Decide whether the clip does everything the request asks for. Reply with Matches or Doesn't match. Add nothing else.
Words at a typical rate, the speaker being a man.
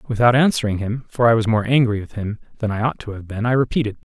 Doesn't match